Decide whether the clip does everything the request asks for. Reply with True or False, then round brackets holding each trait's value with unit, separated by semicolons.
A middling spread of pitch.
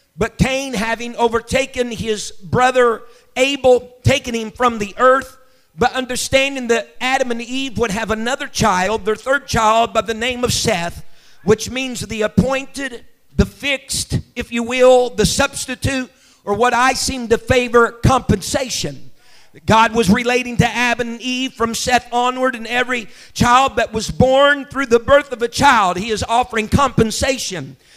False (2.3 semitones)